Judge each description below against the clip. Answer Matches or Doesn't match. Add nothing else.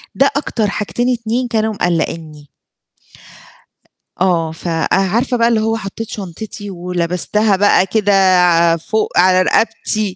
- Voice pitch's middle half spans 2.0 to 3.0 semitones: Doesn't match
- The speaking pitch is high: Matches